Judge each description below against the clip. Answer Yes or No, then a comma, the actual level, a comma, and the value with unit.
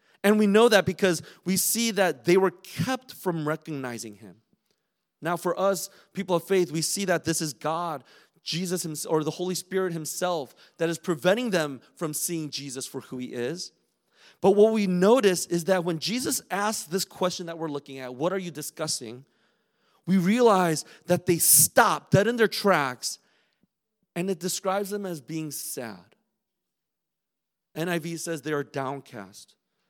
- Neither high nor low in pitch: Yes, medium, 175 Hz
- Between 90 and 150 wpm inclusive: No, average, 170 wpm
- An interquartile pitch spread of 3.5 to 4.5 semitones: Yes, average, 3.8 semitones